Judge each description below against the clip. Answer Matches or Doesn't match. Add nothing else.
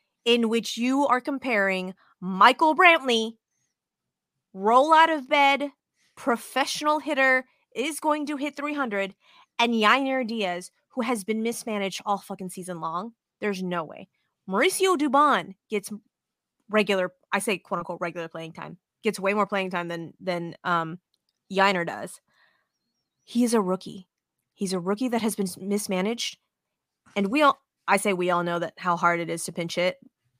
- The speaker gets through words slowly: Doesn't match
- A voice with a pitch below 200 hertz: Doesn't match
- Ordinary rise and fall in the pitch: Doesn't match